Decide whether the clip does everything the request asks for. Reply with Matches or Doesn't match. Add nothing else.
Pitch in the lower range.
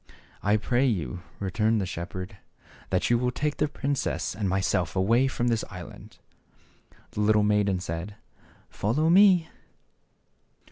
Matches